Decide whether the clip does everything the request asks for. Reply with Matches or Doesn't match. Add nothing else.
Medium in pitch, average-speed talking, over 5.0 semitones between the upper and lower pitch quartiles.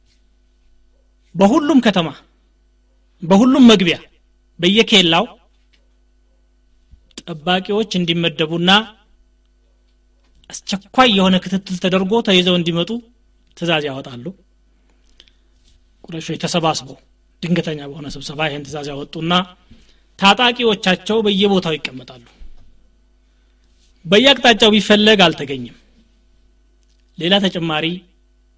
Doesn't match